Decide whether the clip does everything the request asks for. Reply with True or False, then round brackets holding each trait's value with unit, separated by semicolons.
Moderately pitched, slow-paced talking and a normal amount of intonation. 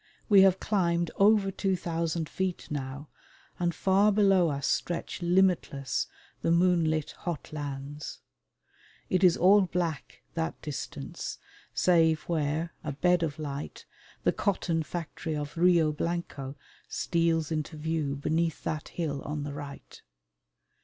True (165 Hz; 130 wpm; 3.1 semitones)